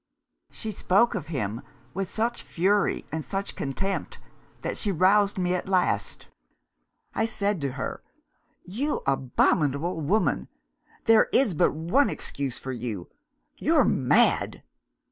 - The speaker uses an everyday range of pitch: No, wide, 6.5 semitones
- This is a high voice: No, medium, 180 Hz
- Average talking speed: No, slow, 125 wpm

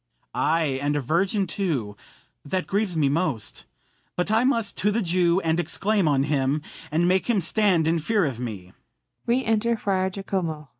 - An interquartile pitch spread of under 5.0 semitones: No, average, 5.3 semitones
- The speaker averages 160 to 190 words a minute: No, average, 150 wpm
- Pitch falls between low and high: Yes, medium, 170 Hz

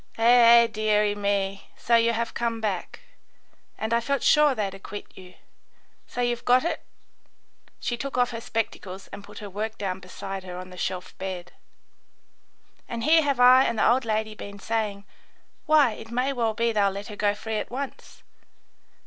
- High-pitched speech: Yes, high, 220 Hz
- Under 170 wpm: No, average, 185 wpm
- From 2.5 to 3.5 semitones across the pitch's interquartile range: Yes, average, 3.1 semitones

